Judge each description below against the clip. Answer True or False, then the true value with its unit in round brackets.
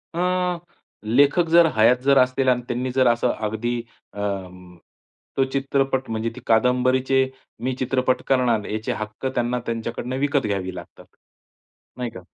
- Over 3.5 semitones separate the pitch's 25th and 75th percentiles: False (3.2 semitones)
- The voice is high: False (125 Hz)